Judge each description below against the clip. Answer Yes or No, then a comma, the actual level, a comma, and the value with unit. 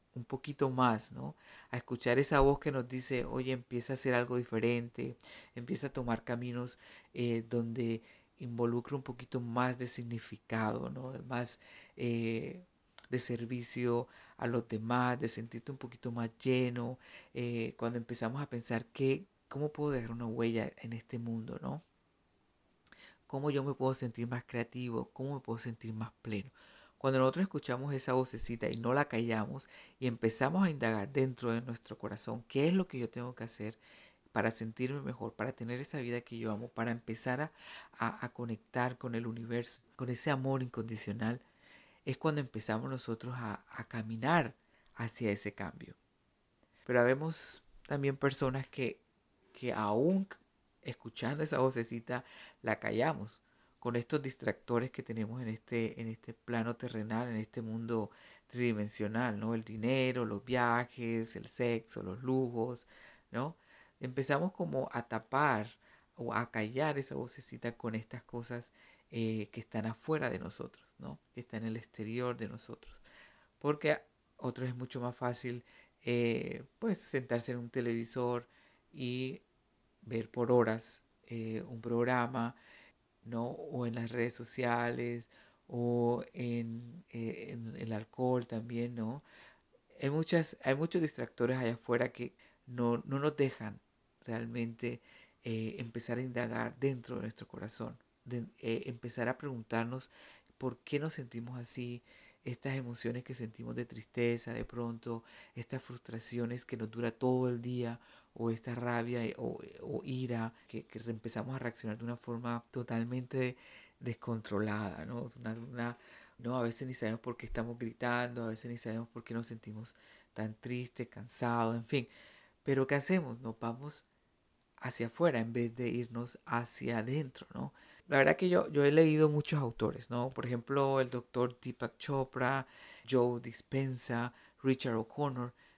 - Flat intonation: Yes, narrow, 1.9 semitones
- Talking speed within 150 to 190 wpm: Yes, average, 155 wpm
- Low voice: Yes, low, 120 Hz